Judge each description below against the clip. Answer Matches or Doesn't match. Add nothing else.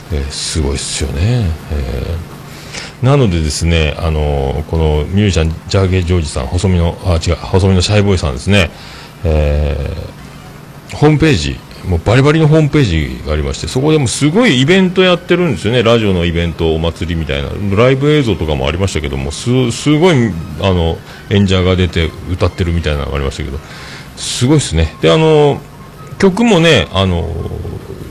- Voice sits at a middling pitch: Doesn't match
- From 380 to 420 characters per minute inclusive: Matches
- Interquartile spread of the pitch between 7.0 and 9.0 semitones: Matches